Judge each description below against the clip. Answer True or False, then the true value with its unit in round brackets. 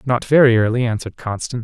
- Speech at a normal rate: True (185 wpm)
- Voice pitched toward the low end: True (120 Hz)